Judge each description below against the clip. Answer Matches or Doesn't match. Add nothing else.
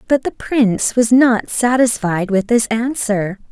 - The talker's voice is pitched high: Matches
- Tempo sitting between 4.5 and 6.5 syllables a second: Doesn't match